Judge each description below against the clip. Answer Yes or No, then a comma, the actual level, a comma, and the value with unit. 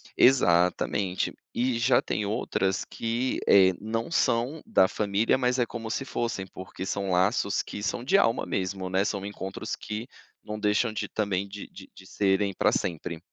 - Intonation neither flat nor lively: Yes, average, 3.5 semitones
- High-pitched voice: No, low, 105 Hz